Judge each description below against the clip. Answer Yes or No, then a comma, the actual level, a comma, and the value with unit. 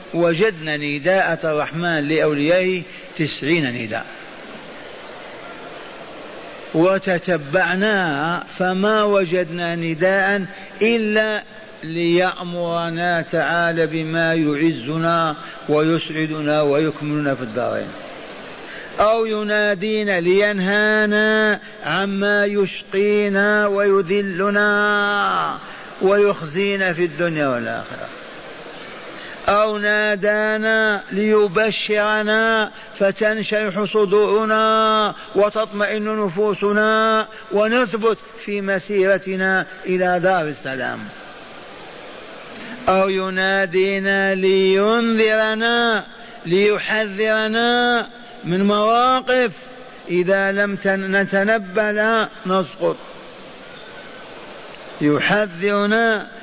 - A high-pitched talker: Yes, high, 200 Hz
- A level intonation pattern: No, average, 3.3 semitones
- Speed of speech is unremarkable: No, slow, 55 wpm